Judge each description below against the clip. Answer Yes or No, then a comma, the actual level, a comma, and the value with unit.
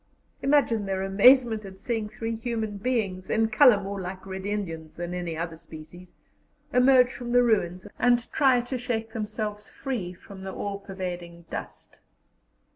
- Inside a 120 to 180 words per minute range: Yes, average, 155 wpm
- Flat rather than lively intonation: No, average, 4.4 semitones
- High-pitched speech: Yes, high, 205 Hz